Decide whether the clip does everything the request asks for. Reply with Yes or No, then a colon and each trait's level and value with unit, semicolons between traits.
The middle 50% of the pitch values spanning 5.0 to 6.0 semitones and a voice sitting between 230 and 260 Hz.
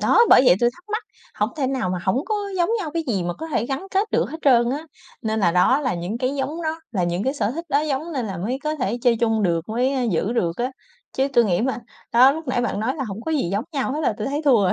Yes: wide, 5.5 semitones; very high, 255 Hz